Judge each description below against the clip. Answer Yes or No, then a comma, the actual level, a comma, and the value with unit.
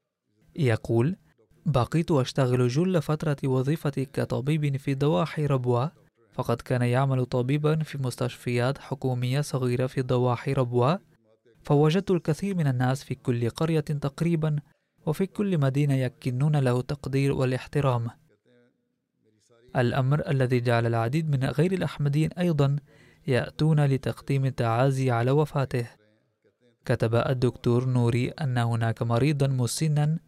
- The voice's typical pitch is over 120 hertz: Yes, low, 135 Hz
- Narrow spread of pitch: No, average, 3.5 semitones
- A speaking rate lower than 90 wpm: No, average, 110 wpm